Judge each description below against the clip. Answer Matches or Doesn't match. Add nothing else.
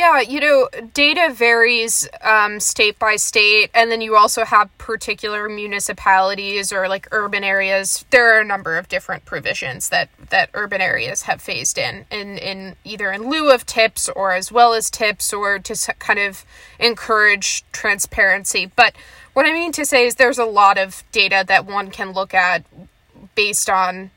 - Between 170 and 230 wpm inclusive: Matches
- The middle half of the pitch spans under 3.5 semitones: Matches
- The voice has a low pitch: Doesn't match